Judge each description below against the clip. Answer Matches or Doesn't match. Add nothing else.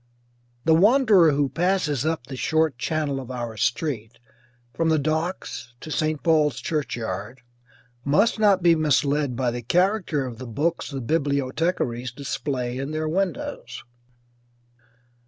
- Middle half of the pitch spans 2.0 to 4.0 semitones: Doesn't match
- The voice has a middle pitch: Matches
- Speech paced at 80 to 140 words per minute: Matches